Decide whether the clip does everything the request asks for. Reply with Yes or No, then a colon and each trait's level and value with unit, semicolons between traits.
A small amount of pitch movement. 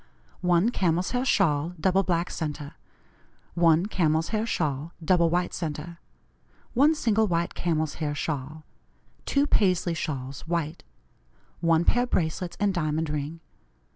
No: average, 3.1 semitones